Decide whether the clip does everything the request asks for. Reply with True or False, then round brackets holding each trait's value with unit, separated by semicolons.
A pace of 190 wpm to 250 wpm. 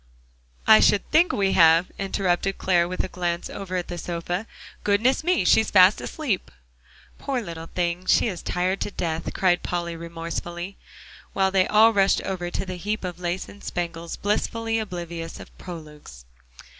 False (165 wpm)